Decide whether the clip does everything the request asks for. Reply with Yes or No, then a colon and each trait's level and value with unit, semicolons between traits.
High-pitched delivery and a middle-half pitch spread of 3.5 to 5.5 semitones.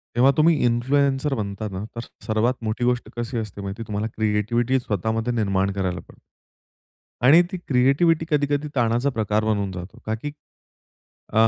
No: low, 115 Hz; average, 4.2 semitones